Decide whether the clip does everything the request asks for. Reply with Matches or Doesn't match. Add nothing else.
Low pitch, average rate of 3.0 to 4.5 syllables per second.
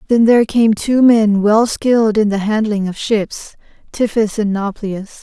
Doesn't match